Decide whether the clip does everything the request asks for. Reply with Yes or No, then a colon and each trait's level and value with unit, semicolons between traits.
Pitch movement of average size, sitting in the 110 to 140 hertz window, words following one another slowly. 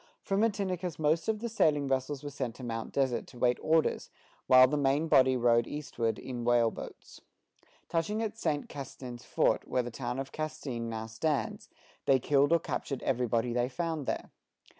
No: average, 4.3 semitones; low, 135 Hz; average, 180 wpm